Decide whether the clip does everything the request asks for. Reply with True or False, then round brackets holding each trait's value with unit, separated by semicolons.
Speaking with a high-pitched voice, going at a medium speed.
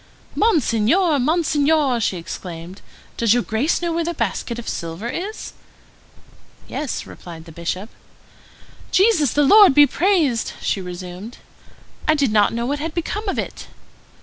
True (270 Hz; 145 wpm)